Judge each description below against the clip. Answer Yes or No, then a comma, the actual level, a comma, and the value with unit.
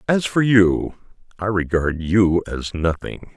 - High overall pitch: No, very low, 95 Hz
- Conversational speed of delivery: Yes, average, 145 wpm